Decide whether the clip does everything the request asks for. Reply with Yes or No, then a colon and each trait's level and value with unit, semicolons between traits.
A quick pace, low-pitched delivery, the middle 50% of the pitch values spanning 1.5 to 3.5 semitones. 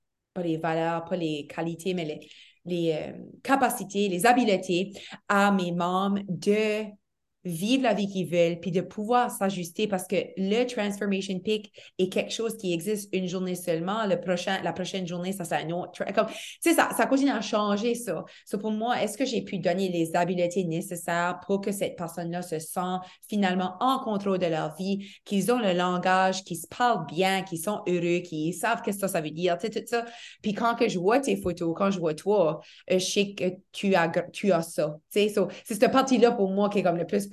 No: fast, 210 wpm; high, 190 Hz; average, 3.2 semitones